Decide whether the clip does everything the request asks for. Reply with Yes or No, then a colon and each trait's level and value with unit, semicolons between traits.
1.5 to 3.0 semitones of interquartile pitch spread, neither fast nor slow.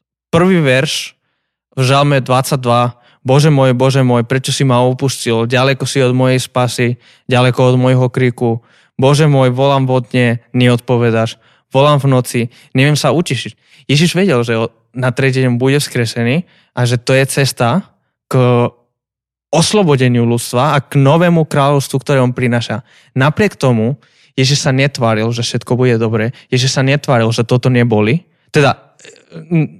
Yes: narrow, 2.4 semitones; average, 145 wpm